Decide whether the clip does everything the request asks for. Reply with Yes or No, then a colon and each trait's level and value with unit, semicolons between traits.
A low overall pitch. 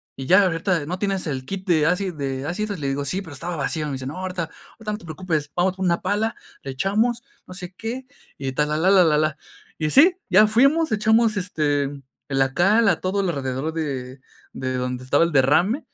No: medium, 175 Hz